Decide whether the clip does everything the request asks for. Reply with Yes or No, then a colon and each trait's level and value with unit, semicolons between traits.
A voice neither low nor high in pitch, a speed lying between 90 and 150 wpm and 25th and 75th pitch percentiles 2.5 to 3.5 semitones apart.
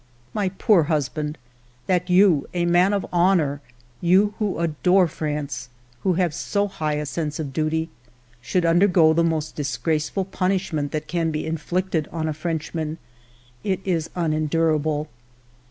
Yes: medium, 160 Hz; average, 145 wpm; average, 3.0 semitones